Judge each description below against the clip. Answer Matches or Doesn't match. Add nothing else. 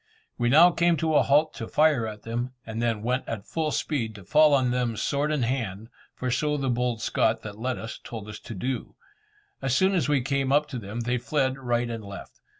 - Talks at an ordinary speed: Doesn't match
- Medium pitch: Doesn't match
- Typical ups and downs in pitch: Matches